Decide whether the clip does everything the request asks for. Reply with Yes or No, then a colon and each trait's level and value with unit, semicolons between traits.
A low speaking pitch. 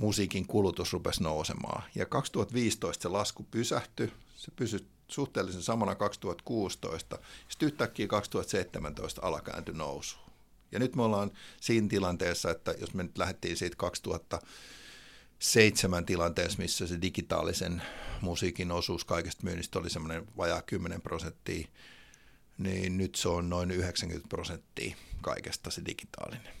Yes: very low, 95 Hz